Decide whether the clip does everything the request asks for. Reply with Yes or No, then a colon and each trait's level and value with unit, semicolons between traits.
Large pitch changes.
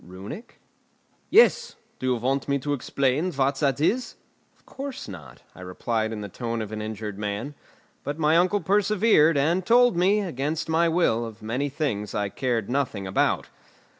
Yes: wide, 7.5 semitones